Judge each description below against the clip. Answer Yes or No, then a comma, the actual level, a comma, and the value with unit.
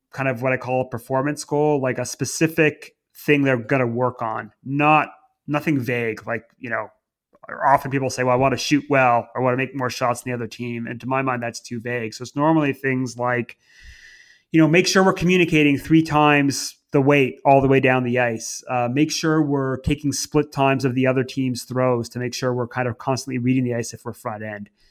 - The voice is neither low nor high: No, low, 130 Hz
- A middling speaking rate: No, fast, 235 wpm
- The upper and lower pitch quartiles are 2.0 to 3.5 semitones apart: Yes, average, 2.9 semitones